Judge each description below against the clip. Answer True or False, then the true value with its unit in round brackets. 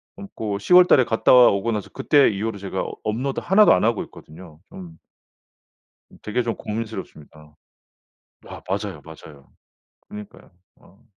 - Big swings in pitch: False (4.4 semitones)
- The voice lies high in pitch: False (105 Hz)